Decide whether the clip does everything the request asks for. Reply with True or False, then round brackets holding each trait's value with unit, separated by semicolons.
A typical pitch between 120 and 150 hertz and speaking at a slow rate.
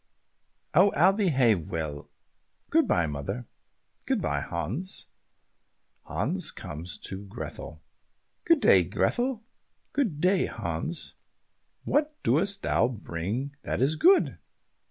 True (135 Hz; 110 wpm)